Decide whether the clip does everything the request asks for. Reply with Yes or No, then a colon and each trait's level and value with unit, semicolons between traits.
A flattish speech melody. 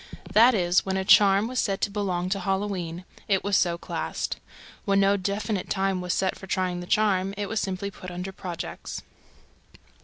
Yes: narrow, 1.7 semitones